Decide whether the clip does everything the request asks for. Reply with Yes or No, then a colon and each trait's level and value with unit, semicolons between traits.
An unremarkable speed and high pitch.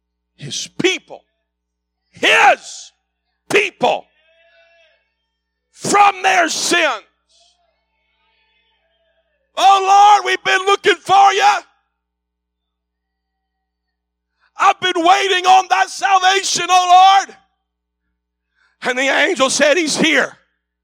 No: slow, 80 wpm; very high, 295 Hz